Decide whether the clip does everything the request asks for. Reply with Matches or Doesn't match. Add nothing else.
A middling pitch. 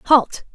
Doesn't match